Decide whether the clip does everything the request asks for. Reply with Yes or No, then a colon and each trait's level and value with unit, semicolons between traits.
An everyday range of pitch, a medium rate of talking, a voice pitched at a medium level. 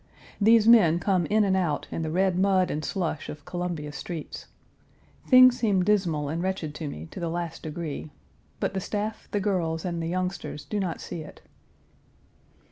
Yes: average, 3.5 semitones; average, 180 wpm; medium, 180 Hz